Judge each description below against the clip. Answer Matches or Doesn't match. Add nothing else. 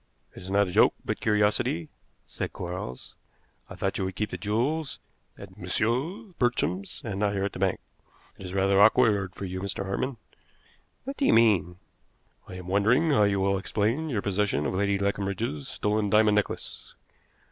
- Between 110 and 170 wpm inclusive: Doesn't match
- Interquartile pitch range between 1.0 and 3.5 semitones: Matches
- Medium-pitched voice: Doesn't match